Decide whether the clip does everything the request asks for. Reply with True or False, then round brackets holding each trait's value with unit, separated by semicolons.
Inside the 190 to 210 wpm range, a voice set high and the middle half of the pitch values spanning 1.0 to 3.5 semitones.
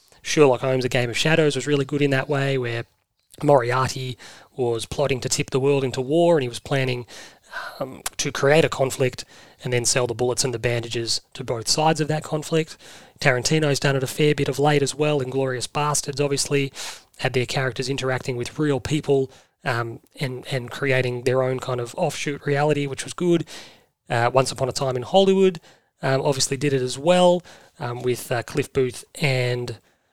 False (195 wpm; 135 Hz; 2.7 semitones)